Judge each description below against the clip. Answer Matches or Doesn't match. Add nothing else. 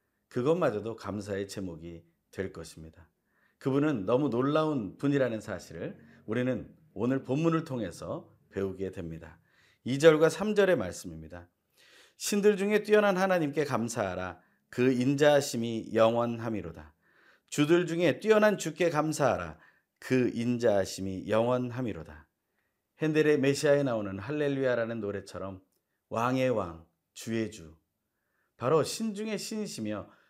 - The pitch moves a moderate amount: Doesn't match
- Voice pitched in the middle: Doesn't match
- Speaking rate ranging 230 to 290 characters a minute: Matches